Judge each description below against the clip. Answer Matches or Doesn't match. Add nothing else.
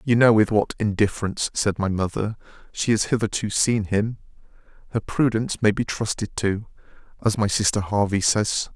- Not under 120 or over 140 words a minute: Doesn't match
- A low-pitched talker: Matches